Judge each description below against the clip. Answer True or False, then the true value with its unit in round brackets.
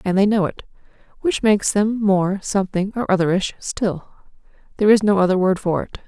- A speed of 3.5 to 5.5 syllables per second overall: False (5.7 syllables/s)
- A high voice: True (195 Hz)